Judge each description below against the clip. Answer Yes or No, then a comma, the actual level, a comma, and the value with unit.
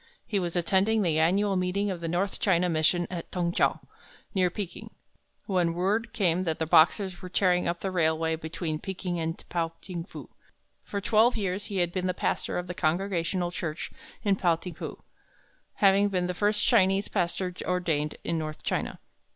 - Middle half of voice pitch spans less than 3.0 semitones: Yes, narrow, 2.5 semitones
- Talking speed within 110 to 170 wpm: No, average, 185 wpm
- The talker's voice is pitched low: No, medium, 180 Hz